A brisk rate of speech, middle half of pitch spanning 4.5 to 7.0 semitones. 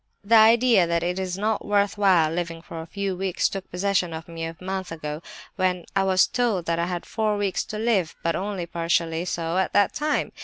No: fast, 220 wpm; average, 3.2 semitones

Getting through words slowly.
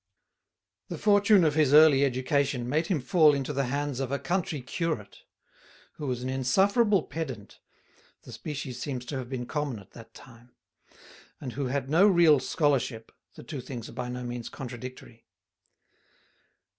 No: average, 160 wpm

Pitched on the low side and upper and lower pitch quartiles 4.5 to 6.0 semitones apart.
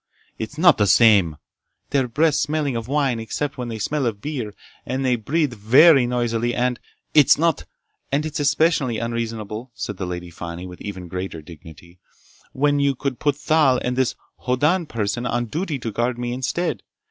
Yes: low, 125 Hz; average, 4.9 semitones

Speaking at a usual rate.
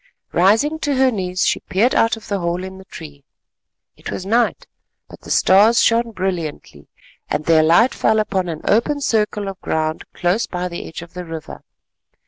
Yes: average, 185 wpm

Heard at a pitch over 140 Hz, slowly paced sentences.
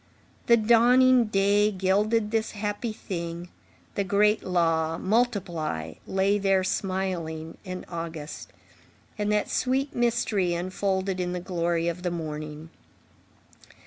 Yes: high, 190 Hz; slow, 115 wpm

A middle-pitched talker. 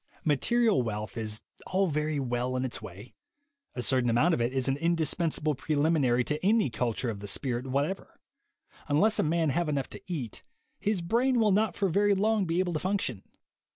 Yes: medium, 150 Hz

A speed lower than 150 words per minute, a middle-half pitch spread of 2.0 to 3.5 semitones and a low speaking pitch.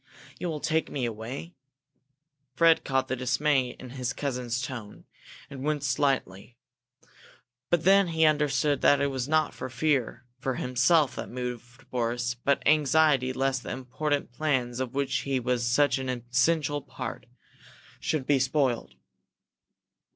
Yes: average, 140 wpm; average, 3.0 semitones; low, 130 Hz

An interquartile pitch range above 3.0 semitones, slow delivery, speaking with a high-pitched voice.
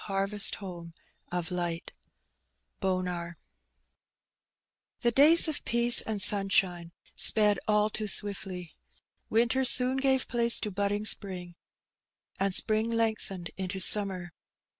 Yes: average, 3.7 semitones; slow, 110 wpm; high, 200 Hz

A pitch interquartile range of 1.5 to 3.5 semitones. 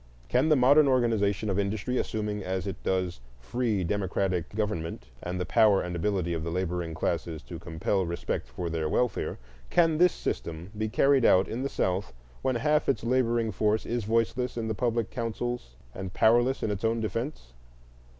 No: average, 5.1 semitones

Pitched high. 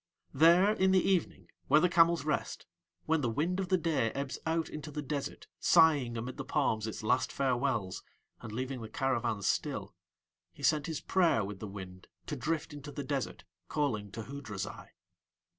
No: medium, 140 Hz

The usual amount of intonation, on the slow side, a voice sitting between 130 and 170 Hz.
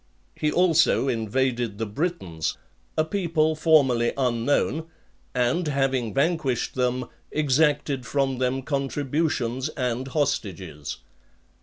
Yes: average, 3.9 semitones; slow, 100 wpm; low, 135 Hz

